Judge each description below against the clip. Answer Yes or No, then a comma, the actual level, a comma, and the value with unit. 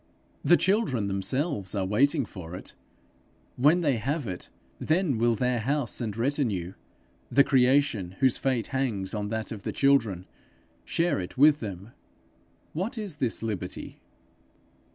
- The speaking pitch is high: No, low, 125 Hz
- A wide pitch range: Yes, wide, 5.9 semitones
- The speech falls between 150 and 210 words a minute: No, average, 140 wpm